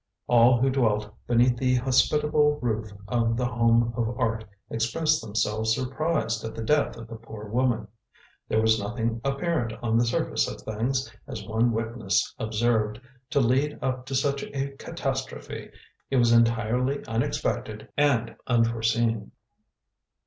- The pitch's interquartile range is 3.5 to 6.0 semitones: No, narrow, 2.6 semitones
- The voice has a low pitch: Yes, low, 115 Hz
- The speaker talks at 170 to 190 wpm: No, average, 140 wpm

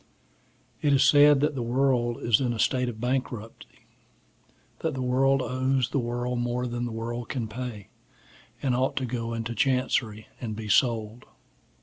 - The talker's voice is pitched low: Yes, low, 125 Hz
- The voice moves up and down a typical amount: No, narrow, 2.1 semitones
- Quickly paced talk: No, average, 165 wpm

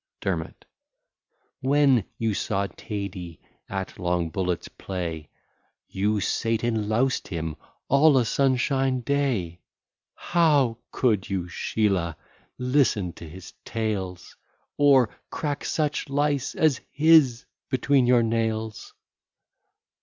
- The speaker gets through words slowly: Yes, slow, 105 wpm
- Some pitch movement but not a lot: No, wide, 6.3 semitones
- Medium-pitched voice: No, low, 115 Hz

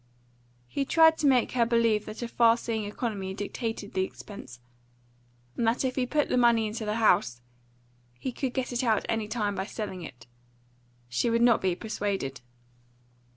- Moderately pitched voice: No, high, 225 Hz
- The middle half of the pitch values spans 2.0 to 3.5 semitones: Yes, average, 3.1 semitones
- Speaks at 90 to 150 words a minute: No, average, 175 wpm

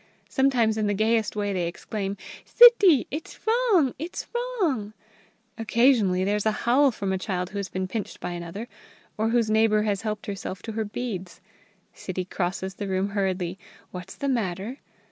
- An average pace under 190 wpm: Yes, average, 170 wpm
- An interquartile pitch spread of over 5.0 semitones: No, average, 4.2 semitones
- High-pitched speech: Yes, high, 210 Hz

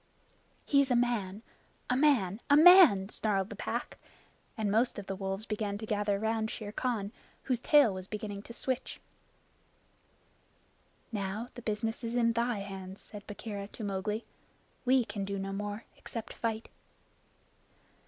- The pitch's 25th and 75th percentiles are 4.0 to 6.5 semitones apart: No, average, 3.1 semitones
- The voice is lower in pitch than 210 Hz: No, high, 215 Hz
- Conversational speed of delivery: Yes, average, 155 wpm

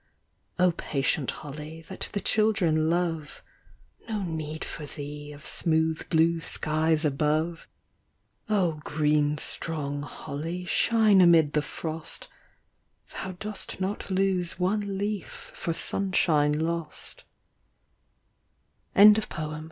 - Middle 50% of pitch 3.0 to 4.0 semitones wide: Yes, average, 3.7 semitones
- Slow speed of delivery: Yes, slow, 105 wpm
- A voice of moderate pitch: Yes, medium, 165 Hz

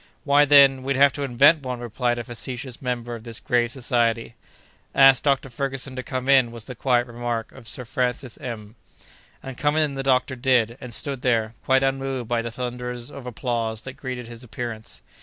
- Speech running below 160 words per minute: No, average, 195 wpm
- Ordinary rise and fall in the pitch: No, narrow, 2.2 semitones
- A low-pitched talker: Yes, low, 125 Hz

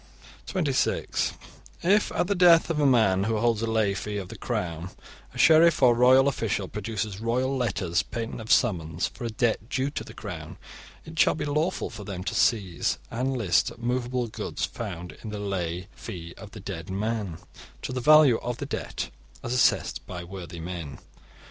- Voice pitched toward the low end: Yes, low, 110 Hz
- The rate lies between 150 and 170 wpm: No, average, 185 wpm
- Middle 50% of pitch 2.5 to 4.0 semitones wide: No, average, 5.2 semitones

